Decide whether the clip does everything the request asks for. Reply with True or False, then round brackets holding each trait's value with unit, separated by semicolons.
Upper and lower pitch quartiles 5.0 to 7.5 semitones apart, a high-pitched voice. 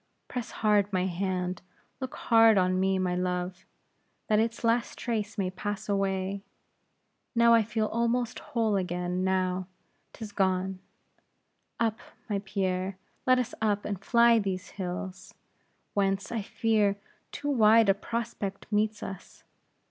False (3.2 semitones; 200 Hz)